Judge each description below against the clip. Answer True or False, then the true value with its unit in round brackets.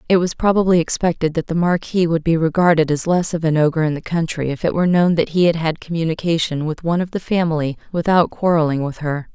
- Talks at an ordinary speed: False (230 wpm)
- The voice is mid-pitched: True (165 Hz)